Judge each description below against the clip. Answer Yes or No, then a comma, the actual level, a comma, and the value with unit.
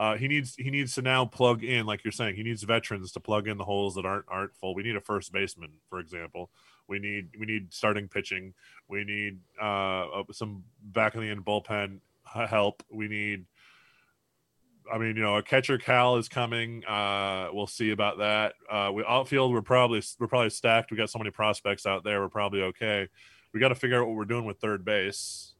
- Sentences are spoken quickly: Yes, fast, 215 wpm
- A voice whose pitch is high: No, low, 105 Hz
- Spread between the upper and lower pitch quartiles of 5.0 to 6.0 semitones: No, narrow, 2.6 semitones